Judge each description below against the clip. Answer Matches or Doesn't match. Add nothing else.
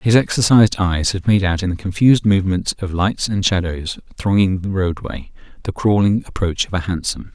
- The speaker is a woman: Doesn't match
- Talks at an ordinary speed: Matches